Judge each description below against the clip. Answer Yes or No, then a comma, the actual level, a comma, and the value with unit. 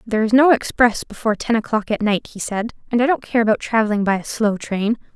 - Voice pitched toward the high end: Yes, high, 220 Hz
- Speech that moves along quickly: Yes, fast, 245 wpm